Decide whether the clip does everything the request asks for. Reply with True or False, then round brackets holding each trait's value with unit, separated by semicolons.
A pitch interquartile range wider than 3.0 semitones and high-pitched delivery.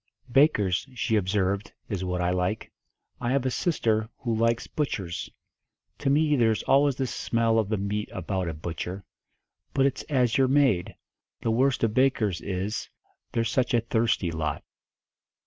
False (5.4 semitones; 110 Hz)